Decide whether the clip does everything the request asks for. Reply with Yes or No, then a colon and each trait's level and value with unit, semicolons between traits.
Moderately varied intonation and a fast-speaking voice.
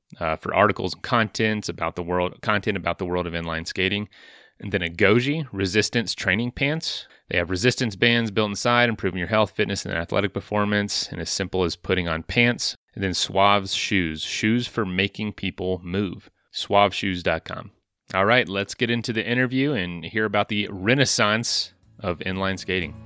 No: average, 3.5 semitones; average, 175 wpm